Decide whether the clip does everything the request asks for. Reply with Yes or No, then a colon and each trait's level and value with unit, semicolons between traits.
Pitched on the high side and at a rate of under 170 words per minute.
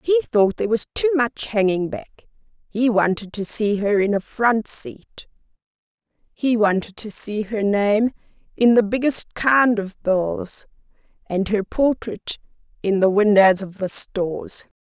Yes: high, 215 Hz; average, 155 wpm